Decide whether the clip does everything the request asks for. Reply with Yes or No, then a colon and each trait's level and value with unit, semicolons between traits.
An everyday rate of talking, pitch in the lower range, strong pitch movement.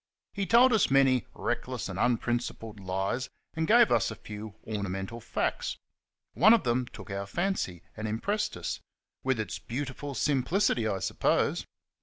Yes: average, 150 wpm; low, 120 Hz; wide, 5.7 semitones